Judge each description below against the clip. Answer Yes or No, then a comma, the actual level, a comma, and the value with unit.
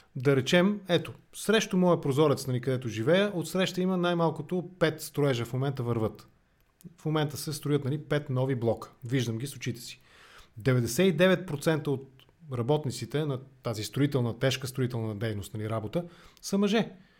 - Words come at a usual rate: Yes, average, 155 wpm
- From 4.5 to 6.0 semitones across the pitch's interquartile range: Yes, wide, 5.4 semitones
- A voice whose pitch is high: No, medium, 140 Hz